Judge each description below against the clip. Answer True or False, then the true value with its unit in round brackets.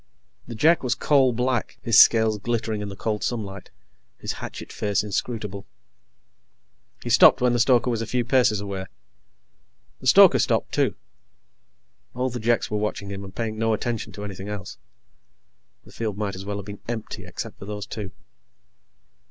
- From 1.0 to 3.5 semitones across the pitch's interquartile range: True (2.8 semitones)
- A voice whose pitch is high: False (110 Hz)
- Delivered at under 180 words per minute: True (170 wpm)